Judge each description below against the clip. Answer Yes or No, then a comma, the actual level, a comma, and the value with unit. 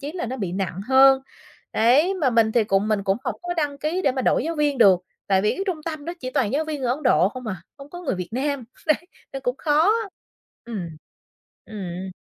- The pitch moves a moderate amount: No, wide, 6.2 semitones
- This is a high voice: Yes, very high, 260 Hz